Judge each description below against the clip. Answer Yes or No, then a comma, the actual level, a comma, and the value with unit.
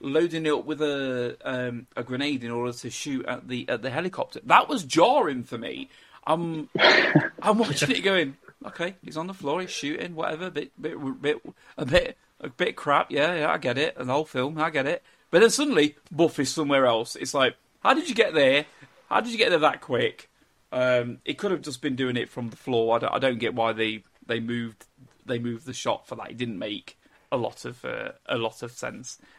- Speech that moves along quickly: Yes, fast, 230 wpm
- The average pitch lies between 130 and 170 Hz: Yes, low, 135 Hz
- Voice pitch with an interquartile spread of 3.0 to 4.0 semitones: No, average, 4.8 semitones